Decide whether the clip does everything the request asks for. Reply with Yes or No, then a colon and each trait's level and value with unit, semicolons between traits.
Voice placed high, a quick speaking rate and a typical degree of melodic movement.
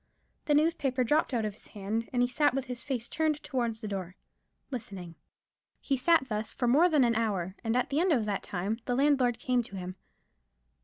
Yes: high, 245 Hz; fast, 210 wpm; average, 4.5 semitones